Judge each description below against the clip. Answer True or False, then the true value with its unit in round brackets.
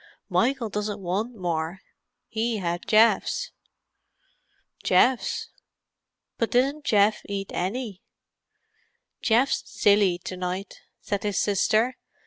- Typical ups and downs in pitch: True (3.5 semitones)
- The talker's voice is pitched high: True (210 Hz)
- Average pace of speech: False (100 wpm)